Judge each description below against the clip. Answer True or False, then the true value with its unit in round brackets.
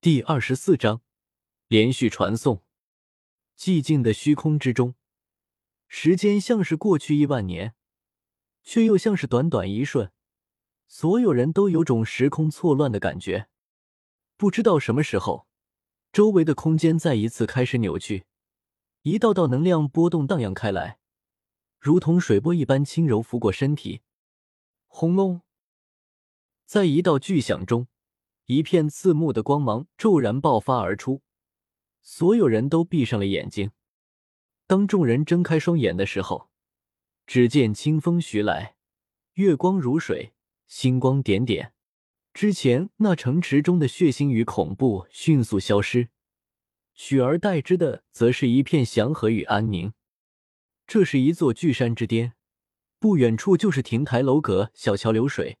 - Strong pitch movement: True (7.2 semitones)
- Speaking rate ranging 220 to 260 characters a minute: False (210 characters per minute)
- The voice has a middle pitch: False (130 Hz)